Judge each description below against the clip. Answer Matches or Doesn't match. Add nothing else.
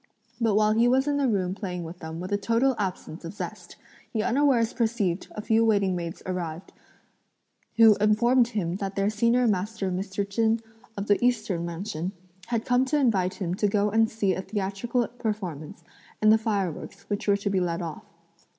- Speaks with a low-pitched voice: Doesn't match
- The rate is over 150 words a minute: Matches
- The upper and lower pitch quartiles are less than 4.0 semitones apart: Matches